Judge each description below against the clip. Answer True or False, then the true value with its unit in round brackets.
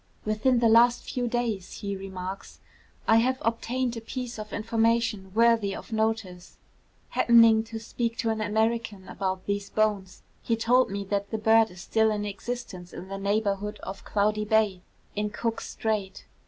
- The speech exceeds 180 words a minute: False (165 wpm)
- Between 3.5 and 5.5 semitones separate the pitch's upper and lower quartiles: False (2.4 semitones)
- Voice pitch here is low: False (220 Hz)